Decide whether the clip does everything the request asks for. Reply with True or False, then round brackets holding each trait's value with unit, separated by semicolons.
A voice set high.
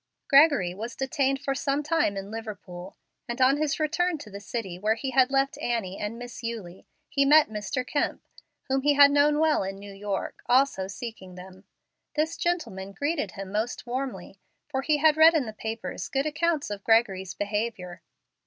True (240 Hz)